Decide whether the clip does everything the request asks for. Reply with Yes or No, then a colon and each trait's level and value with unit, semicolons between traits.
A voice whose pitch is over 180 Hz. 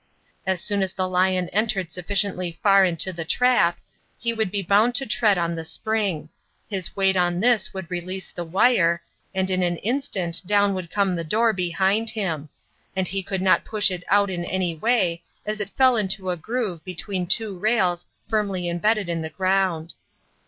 Yes: high, 190 Hz